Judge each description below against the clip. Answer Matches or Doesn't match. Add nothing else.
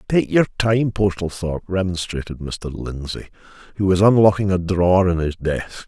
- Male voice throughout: Matches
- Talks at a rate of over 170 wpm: Doesn't match